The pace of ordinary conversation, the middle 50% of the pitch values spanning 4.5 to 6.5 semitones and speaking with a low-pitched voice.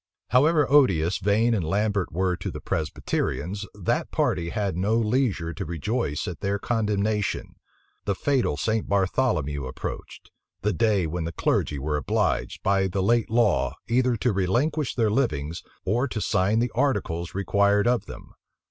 Yes: average, 155 wpm; average, 5.0 semitones; low, 100 Hz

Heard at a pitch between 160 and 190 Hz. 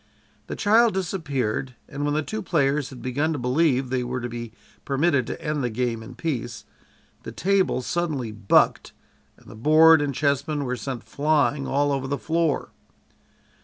No: medium, 140 Hz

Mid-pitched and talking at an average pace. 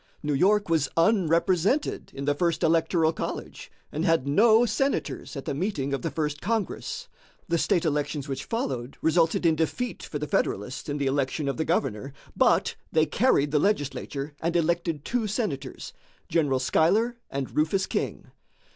Yes: medium, 160 Hz; average, 165 wpm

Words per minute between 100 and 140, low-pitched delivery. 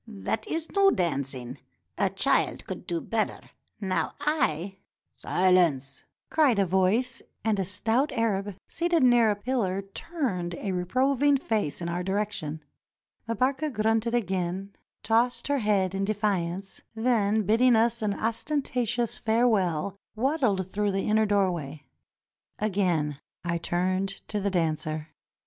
No: slow, 135 wpm; high, 205 Hz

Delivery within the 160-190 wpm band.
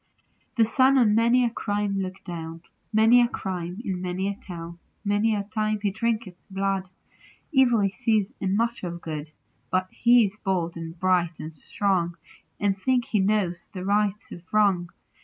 Yes: average, 175 wpm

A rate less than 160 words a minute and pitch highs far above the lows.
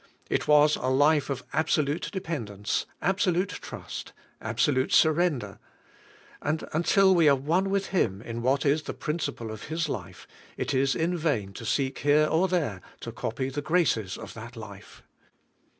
No: average, 165 wpm; wide, 5.7 semitones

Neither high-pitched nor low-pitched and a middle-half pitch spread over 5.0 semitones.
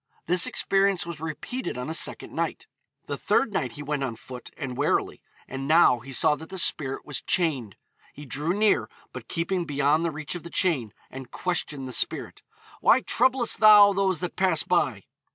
Yes: medium, 160 Hz; wide, 5.4 semitones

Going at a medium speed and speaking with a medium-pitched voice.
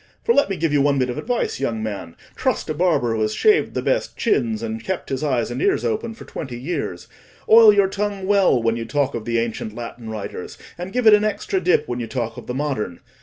No: fast, 235 wpm; medium, 145 Hz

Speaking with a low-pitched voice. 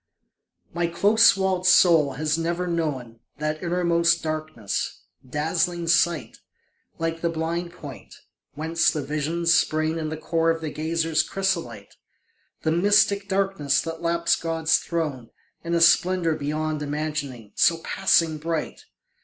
No: medium, 165 Hz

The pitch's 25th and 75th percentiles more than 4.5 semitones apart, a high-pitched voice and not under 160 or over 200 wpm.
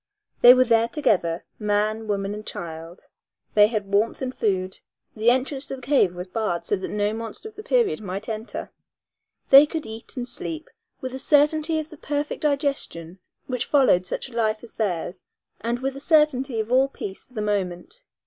Yes: average, 5.1 semitones; high, 230 Hz; average, 190 wpm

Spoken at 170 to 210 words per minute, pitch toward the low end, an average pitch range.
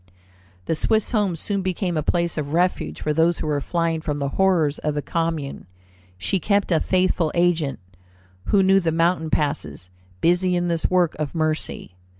No: average, 175 wpm; medium, 165 Hz; average, 3.1 semitones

